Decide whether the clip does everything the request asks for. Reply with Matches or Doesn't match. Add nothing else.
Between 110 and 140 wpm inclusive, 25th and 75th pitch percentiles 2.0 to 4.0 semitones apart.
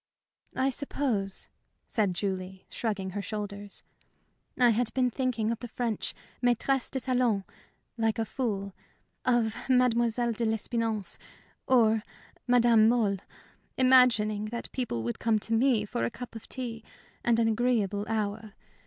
Matches